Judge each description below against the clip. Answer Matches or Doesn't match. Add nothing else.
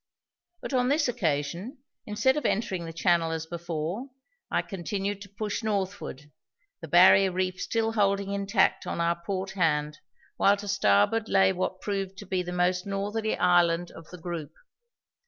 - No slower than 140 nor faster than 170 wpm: Matches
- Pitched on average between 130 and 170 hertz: Doesn't match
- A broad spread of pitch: Doesn't match